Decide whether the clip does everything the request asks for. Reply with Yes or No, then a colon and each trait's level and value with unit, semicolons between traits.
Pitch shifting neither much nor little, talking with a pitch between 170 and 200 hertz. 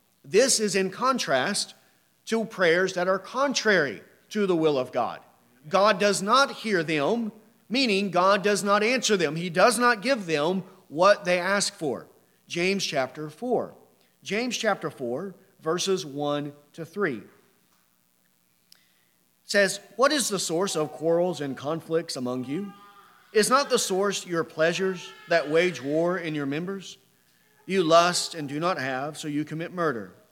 Yes: average, 4.8 semitones; medium, 185 Hz